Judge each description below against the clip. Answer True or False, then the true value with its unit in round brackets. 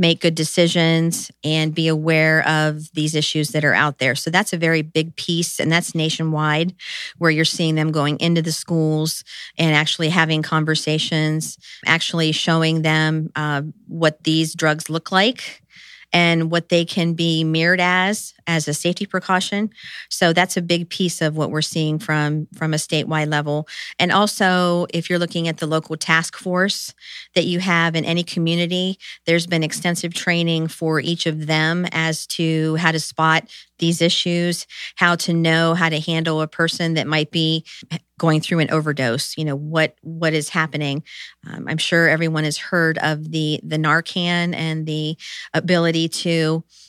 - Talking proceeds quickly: False (170 wpm)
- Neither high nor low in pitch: True (160 Hz)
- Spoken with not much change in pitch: True (1.5 semitones)